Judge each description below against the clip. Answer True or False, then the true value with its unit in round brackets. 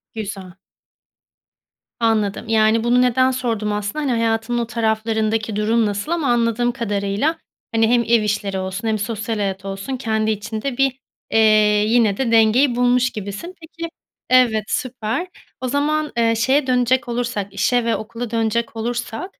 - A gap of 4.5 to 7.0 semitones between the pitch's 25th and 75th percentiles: False (2.4 semitones)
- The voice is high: True (230 Hz)